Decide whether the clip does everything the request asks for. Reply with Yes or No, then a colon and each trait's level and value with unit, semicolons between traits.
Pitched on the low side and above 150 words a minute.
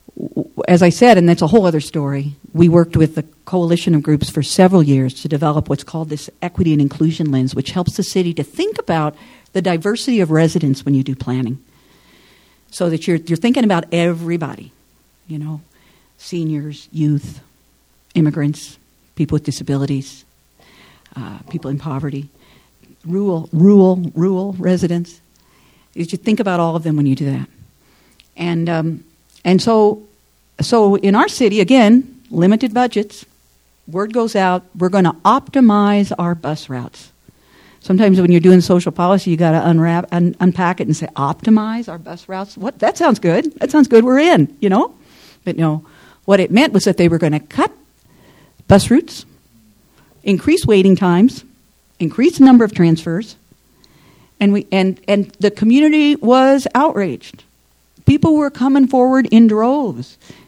No: medium, 175 Hz; average, 160 wpm